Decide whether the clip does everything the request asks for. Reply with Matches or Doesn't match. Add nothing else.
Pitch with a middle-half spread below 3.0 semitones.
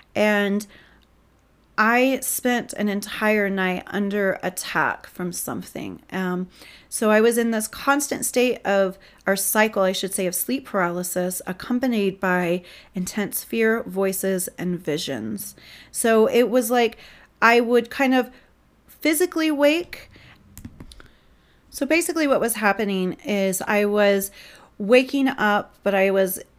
Doesn't match